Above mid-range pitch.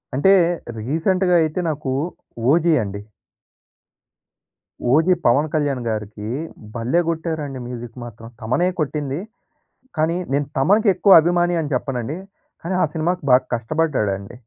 No: medium, 150 Hz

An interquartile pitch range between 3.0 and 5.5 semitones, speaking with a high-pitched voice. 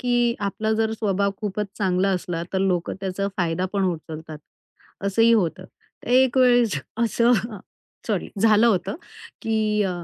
Yes: average, 3.5 semitones; high, 205 Hz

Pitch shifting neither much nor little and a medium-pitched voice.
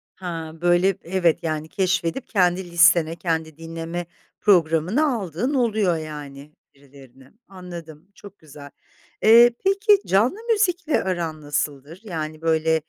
Yes: average, 3.8 semitones; medium, 170 Hz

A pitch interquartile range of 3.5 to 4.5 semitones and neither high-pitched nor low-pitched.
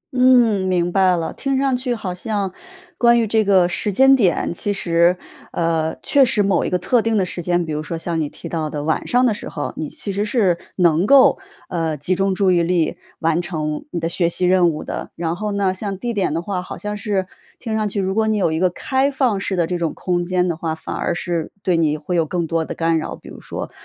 Yes: average, 3.9 semitones; medium, 180 Hz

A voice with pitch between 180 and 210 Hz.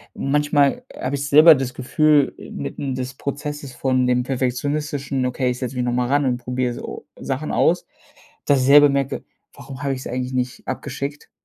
No: low, 135 Hz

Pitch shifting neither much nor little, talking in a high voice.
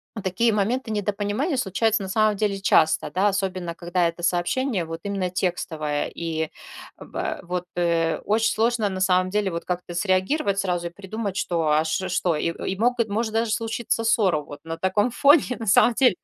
Yes: average, 4.0 semitones; high, 195 Hz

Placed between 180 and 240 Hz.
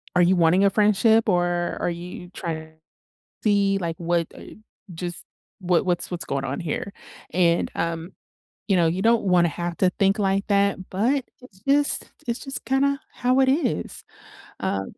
Yes: medium, 185 Hz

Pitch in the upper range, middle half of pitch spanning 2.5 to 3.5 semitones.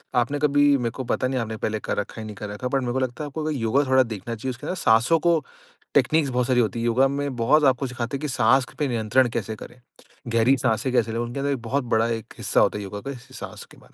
No: low, 125 Hz; average, 3.1 semitones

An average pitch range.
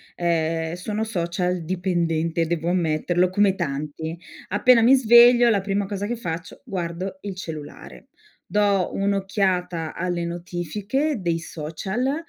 Yes: average, 3.4 semitones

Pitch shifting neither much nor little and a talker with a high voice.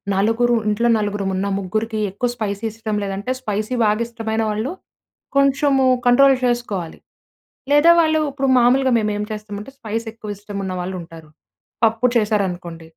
Yes: average, 3.2 semitones; high, 215 Hz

